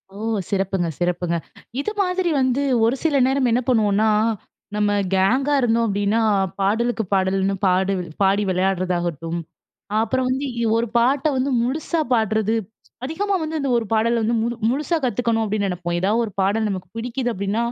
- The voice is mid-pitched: No, high, 225 Hz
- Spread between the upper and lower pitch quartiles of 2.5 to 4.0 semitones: No, average, 4.9 semitones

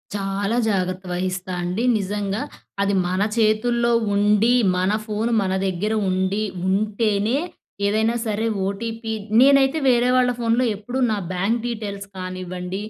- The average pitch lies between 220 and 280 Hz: No, high, 205 Hz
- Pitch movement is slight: No, average, 3.3 semitones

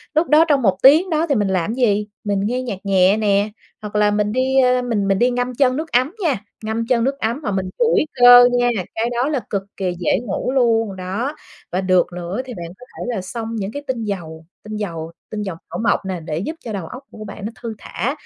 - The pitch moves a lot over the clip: No, average, 4.4 semitones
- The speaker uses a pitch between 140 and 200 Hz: No, high, 220 Hz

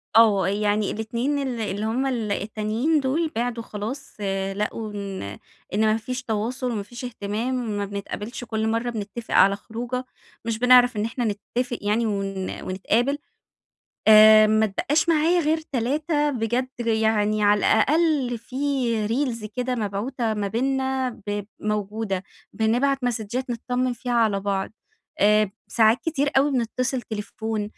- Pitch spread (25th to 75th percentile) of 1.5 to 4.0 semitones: Yes, average, 3.3 semitones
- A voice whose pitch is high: Yes, high, 230 Hz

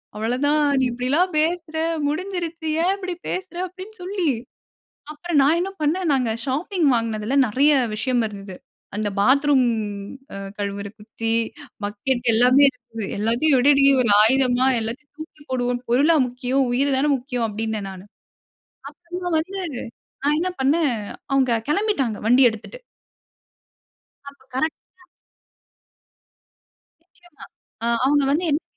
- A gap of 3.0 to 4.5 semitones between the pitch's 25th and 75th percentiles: No, average, 5.1 semitones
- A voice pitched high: Yes, very high, 270 Hz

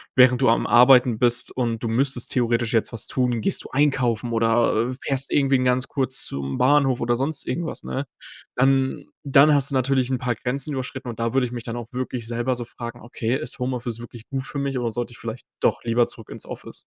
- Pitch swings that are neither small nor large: No, narrow, 2.2 semitones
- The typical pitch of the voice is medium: No, low, 125 Hz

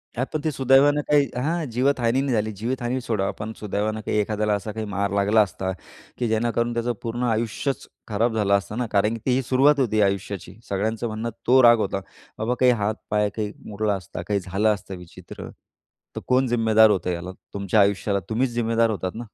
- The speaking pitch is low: Yes, low, 110 Hz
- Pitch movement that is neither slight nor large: Yes, average, 3.1 semitones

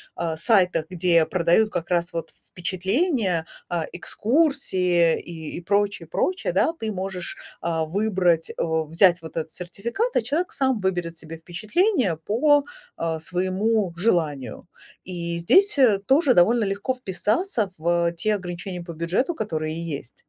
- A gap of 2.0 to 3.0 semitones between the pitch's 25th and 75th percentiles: No, average, 4.7 semitones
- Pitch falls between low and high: Yes, medium, 180 Hz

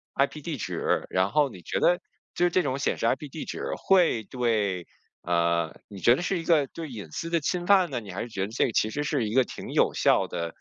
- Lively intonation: Yes, wide, 8.2 semitones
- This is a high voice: No, low, 130 Hz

